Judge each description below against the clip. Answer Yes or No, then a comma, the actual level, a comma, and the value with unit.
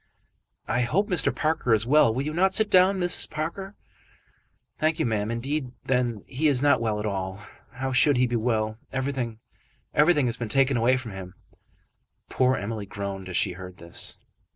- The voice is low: Yes, low, 125 Hz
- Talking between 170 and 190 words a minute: Yes, average, 180 wpm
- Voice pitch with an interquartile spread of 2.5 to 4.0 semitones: No, wide, 5.5 semitones